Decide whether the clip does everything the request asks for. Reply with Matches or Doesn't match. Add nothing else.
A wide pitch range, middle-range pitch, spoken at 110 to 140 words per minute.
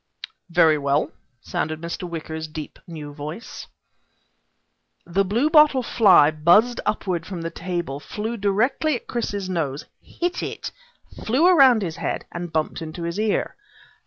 Matches